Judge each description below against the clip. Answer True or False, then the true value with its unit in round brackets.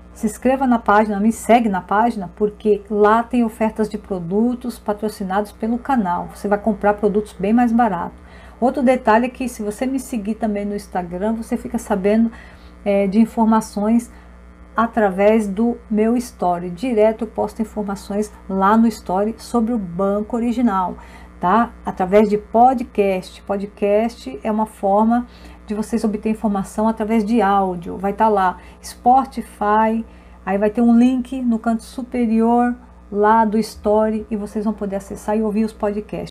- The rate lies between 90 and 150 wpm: False (160 wpm)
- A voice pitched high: True (215 Hz)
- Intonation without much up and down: True (2.1 semitones)